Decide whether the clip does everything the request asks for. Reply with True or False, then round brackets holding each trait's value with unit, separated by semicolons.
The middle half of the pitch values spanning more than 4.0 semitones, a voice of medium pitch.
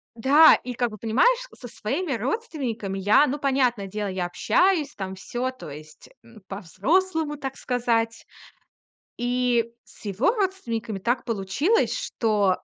False (5.6 semitones; 240 Hz)